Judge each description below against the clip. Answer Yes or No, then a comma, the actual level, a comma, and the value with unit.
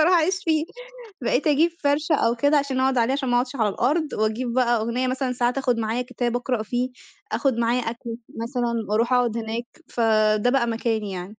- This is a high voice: Yes, high, 245 Hz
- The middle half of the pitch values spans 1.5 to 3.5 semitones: Yes, average, 2.7 semitones